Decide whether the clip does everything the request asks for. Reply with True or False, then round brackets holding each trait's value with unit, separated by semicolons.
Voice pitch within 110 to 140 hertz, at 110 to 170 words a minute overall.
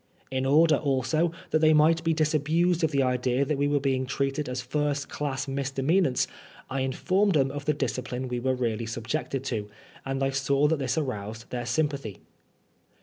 False (135 Hz; 185 wpm)